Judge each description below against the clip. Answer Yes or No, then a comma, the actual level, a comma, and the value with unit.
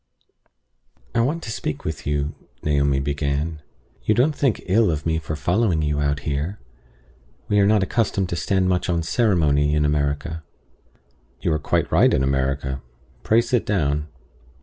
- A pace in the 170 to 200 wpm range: No, average, 160 wpm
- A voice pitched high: No, very low, 80 Hz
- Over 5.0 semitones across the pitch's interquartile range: Yes, wide, 5.6 semitones